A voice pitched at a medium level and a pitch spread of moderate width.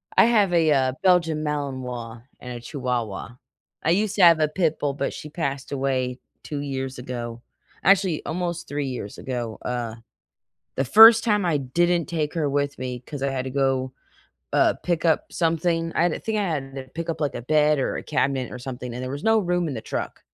Yes: medium, 145 Hz; average, 4.7 semitones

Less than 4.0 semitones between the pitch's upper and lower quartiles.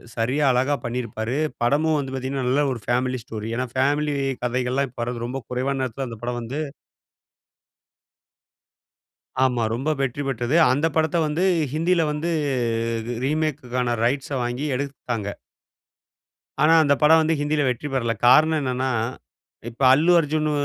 Yes: average, 3.4 semitones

